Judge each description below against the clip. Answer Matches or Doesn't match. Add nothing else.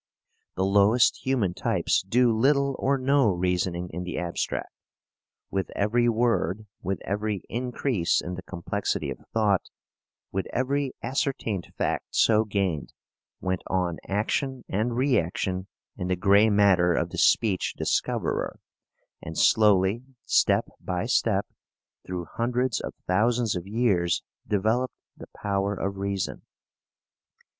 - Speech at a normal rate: Doesn't match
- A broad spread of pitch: Doesn't match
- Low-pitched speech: Matches